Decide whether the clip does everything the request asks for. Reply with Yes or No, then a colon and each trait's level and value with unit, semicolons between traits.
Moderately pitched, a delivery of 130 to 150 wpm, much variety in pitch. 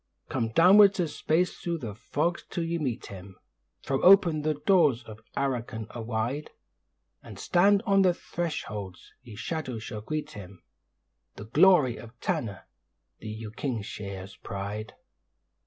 No: low, 130 Hz; slow, 135 wpm; wide, 7.6 semitones